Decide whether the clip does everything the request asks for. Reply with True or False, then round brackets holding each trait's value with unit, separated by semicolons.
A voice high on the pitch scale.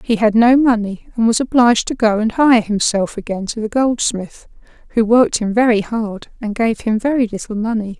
True (225 Hz)